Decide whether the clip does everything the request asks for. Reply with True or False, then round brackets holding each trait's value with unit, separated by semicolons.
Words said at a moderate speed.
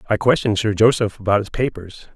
True (195 wpm)